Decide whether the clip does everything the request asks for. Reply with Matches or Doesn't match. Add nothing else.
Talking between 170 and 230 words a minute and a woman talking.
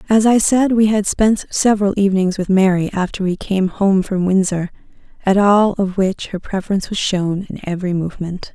Matches